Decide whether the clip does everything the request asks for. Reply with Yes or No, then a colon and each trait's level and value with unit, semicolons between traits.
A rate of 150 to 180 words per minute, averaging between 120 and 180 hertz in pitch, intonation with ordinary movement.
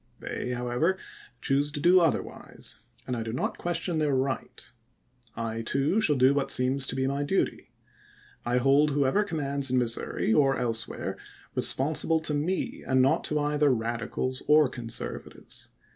Yes: average, 170 wpm; low, 135 Hz; average, 3.2 semitones